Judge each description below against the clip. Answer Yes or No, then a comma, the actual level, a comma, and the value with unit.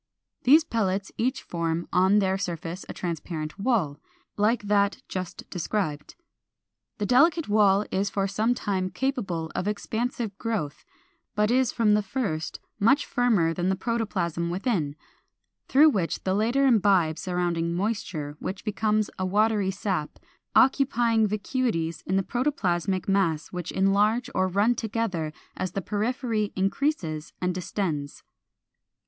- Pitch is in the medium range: No, high, 200 Hz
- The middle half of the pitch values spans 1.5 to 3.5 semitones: No, average, 4.3 semitones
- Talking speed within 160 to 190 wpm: No, slow, 135 wpm